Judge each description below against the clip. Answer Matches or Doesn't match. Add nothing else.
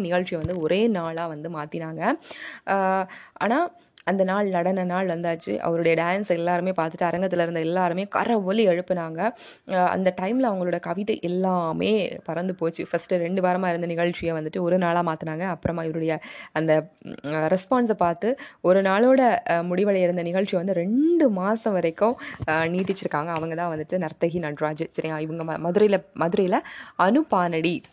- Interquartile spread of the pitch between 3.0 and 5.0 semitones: Doesn't match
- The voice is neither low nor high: Matches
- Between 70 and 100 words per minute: Doesn't match